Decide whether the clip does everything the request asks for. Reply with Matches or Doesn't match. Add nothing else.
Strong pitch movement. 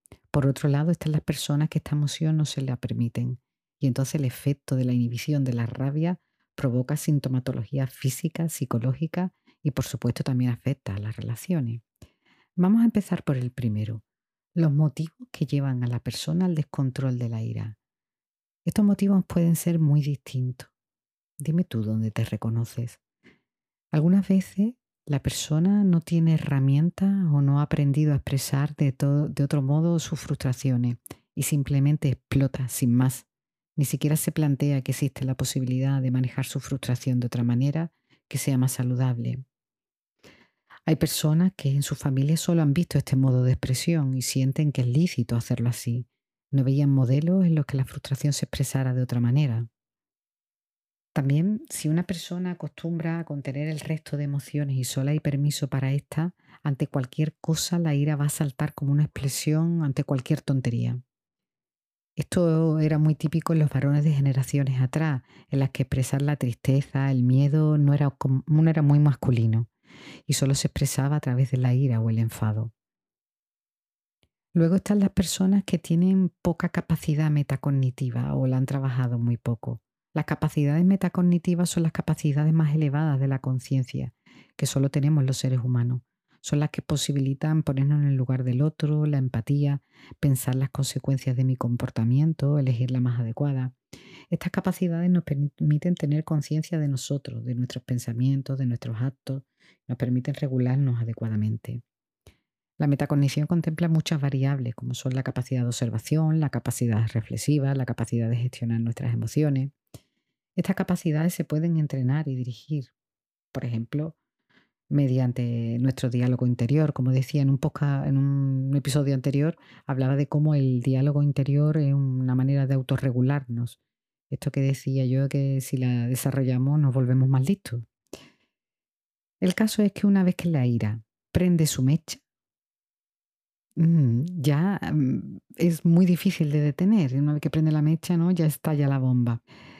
Doesn't match